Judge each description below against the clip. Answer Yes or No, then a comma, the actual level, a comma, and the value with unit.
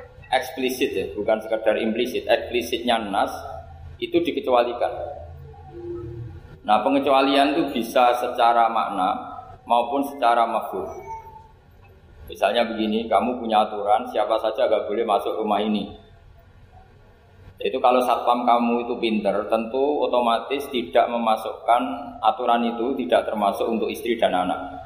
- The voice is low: Yes, low, 115 Hz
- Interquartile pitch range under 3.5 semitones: Yes, narrow, 2.5 semitones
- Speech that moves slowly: No, average, 115 wpm